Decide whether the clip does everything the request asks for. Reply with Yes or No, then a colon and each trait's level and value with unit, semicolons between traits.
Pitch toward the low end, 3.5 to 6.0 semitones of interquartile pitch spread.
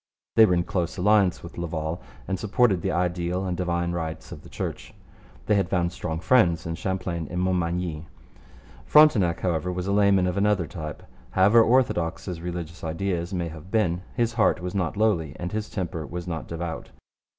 No: very low, 90 Hz; narrow, 2.6 semitones